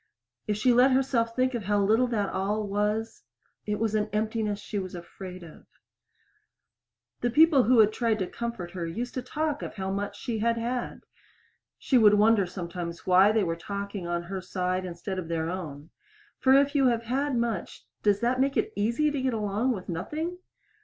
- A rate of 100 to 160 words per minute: No, average, 195 wpm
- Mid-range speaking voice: No, high, 210 Hz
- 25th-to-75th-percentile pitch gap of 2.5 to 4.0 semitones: No, average, 4.4 semitones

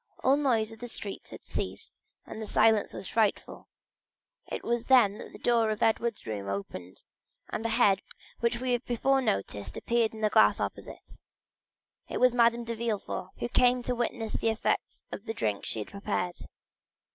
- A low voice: No, high, 225 Hz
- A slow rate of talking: No, average, 180 wpm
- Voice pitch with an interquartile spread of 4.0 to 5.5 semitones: No, average, 3.0 semitones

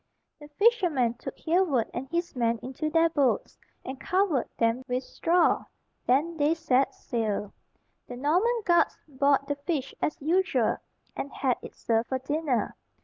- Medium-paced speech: Yes, average, 150 wpm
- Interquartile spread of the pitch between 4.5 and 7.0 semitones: Yes, average, 4.8 semitones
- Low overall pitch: No, very high, 285 Hz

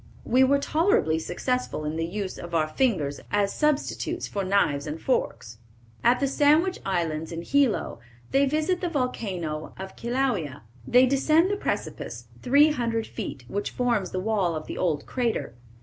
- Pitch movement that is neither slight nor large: No, wide, 8.7 semitones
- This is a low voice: No, high, 220 Hz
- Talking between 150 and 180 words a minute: Yes, average, 165 wpm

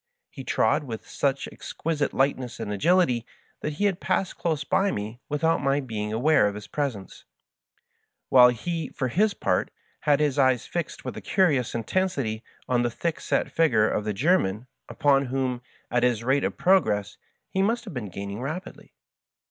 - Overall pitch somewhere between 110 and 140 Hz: Yes, low, 135 Hz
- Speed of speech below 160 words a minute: No, average, 175 wpm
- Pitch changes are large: Yes, wide, 6.2 semitones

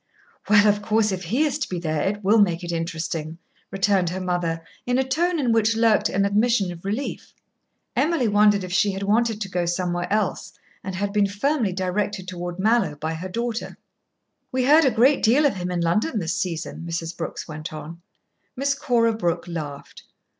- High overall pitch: Yes, high, 200 Hz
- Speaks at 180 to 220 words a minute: Yes, average, 195 wpm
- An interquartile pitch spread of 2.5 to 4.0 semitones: No, average, 4.5 semitones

